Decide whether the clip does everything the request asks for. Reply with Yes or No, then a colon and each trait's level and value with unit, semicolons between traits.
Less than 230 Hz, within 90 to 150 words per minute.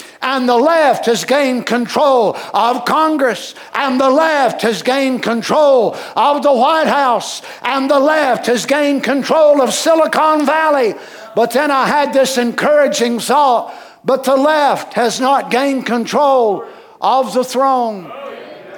No: very high, 265 Hz; average, 140 wpm